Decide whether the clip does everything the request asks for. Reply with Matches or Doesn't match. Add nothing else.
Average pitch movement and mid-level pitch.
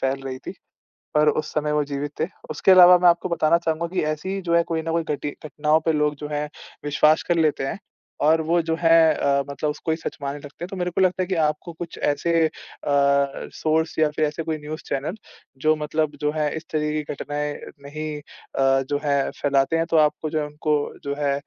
Doesn't match